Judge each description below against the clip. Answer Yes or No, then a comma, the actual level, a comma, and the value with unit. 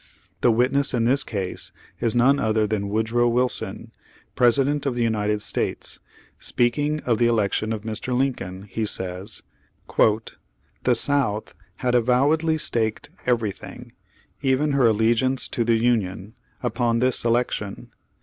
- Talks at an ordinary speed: No, slow, 130 wpm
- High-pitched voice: No, low, 120 Hz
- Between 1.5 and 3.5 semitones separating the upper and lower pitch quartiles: Yes, average, 2.8 semitones